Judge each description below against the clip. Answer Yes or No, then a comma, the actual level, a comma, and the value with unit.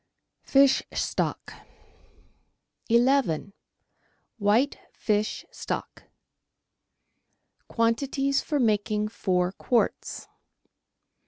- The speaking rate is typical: No, slow, 60 wpm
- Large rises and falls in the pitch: No, average, 4.7 semitones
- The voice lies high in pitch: Yes, high, 230 Hz